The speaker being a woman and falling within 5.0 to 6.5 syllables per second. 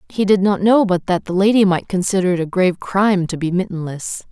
Yes: female; 5.9 syllables/s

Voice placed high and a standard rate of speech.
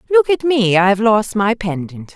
Yes: high, 220 Hz; average, 165 wpm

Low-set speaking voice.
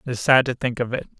Yes: low, 125 Hz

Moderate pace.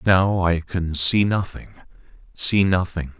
No: slow, 115 wpm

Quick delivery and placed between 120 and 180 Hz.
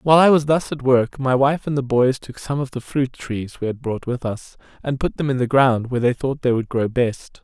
Yes: fast, 280 wpm; low, 130 Hz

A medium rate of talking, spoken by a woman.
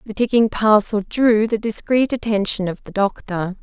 Yes: average, 165 wpm; female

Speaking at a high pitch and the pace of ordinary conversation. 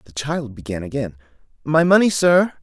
No: medium, 140 Hz; average, 160 wpm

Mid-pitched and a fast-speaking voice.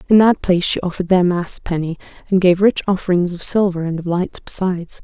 Yes: medium, 180 Hz; fast, 215 wpm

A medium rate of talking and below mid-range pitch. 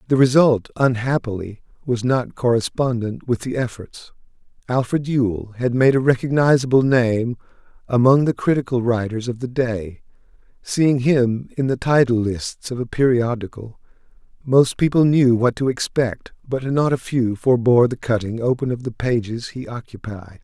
Yes: average, 150 wpm; low, 125 Hz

